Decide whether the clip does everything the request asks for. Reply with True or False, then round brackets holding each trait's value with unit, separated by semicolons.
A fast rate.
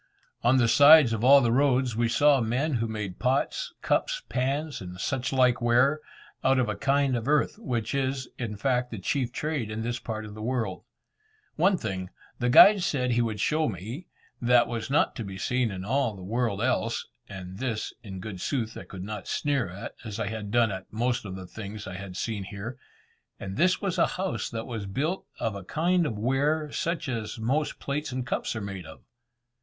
True (210 wpm)